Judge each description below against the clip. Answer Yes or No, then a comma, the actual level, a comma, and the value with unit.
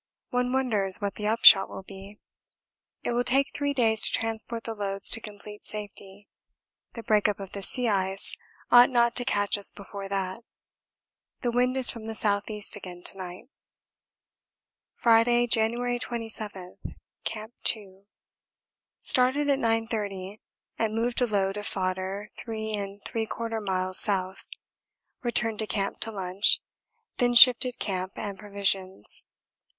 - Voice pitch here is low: No, high, 215 Hz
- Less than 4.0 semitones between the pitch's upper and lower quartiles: Yes, average, 3.1 semitones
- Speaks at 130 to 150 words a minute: Yes, average, 140 wpm